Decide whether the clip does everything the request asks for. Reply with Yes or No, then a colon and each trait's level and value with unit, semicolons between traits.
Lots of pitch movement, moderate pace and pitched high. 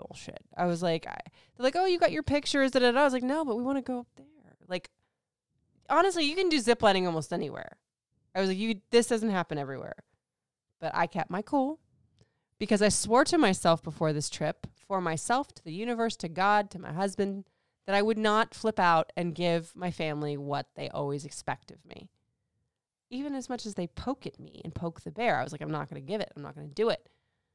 No: wide, 7.2 semitones; fast, 225 wpm; high, 195 Hz